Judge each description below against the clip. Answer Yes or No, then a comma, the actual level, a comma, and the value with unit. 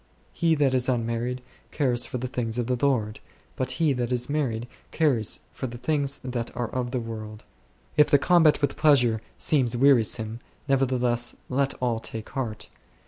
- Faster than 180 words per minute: No, average, 175 wpm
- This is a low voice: Yes, low, 125 Hz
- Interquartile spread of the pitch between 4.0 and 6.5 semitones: No, average, 2.8 semitones